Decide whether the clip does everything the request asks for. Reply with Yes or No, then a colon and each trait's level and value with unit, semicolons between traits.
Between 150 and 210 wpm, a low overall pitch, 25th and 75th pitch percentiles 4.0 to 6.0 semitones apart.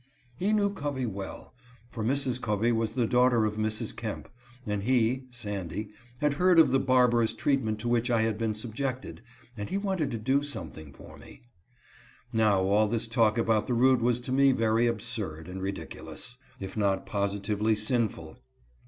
No: average, 170 wpm; low, 115 Hz; average, 3.3 semitones